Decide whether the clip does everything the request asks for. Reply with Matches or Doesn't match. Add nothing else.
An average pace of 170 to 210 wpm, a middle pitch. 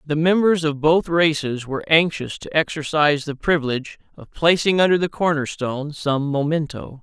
Doesn't match